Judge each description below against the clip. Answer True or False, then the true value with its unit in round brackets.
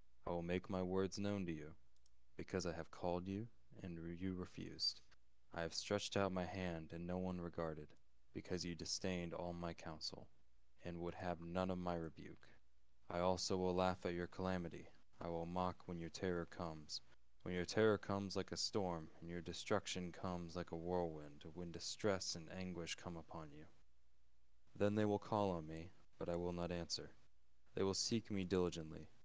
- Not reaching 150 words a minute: False (185 wpm)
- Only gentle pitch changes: True (2.3 semitones)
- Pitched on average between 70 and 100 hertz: True (85 Hz)